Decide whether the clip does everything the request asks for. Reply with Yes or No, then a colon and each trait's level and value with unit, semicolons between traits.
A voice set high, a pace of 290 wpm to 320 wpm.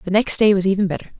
Yes: high, 195 Hz; fast, 300 wpm